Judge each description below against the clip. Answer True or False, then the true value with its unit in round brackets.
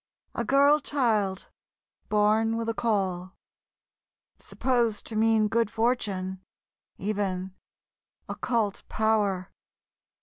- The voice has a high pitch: True (215 Hz)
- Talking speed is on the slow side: True (90 wpm)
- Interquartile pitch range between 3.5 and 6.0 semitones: False (2.9 semitones)